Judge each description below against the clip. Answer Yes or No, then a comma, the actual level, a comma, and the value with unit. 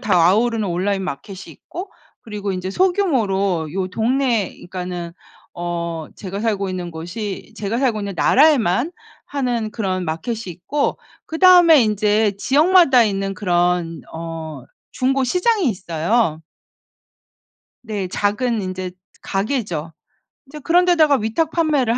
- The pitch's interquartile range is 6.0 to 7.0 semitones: Yes, wide, 6.3 semitones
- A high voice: Yes, high, 210 Hz